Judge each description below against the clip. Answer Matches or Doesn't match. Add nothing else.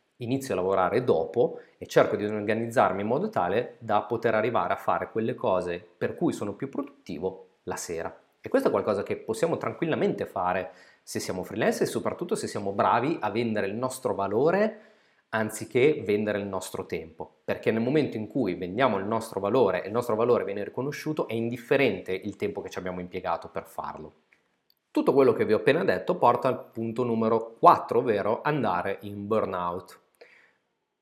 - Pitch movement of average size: Matches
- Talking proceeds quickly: Matches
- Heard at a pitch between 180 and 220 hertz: Doesn't match